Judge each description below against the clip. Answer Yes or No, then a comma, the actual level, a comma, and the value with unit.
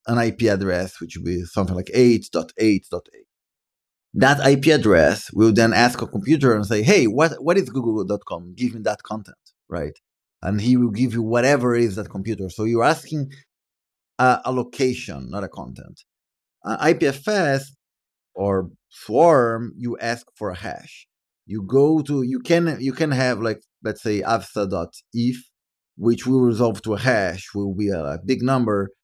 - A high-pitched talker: No, low, 115 Hz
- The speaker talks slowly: No, average, 165 wpm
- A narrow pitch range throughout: No, average, 4.2 semitones